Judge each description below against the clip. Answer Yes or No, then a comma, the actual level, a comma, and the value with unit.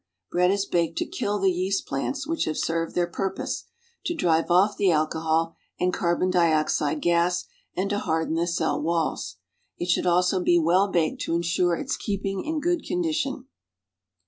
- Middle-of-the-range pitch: Yes, medium, 175 Hz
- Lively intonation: No, average, 2.9 semitones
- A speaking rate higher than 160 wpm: Yes, average, 170 wpm